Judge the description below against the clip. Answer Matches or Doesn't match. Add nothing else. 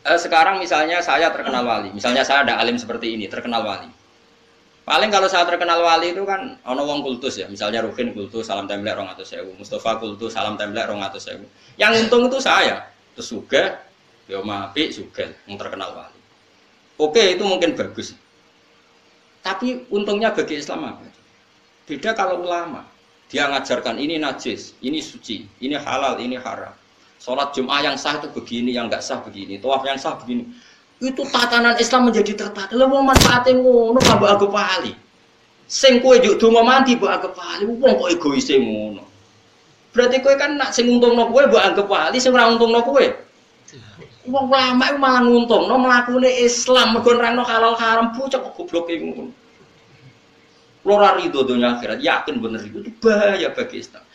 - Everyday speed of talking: Doesn't match